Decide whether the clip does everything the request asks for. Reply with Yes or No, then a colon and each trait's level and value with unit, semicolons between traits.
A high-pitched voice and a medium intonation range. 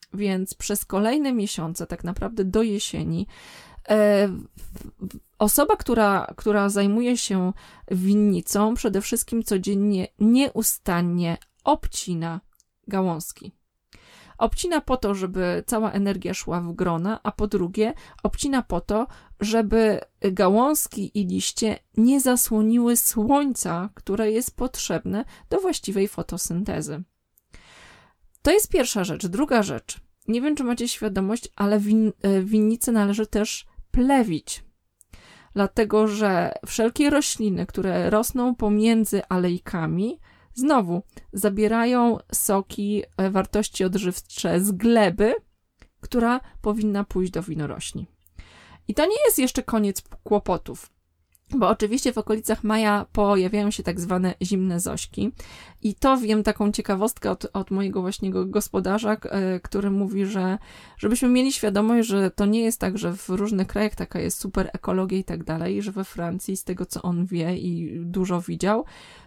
Yes: high, 205 Hz; average, 3.1 semitones